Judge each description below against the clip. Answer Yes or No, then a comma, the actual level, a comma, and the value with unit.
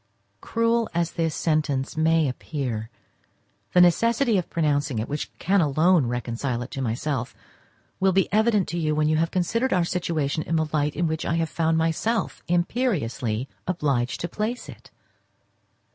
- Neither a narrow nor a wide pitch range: Yes, average, 4.3 semitones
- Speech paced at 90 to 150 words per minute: No, average, 160 wpm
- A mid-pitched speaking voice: Yes, medium, 160 Hz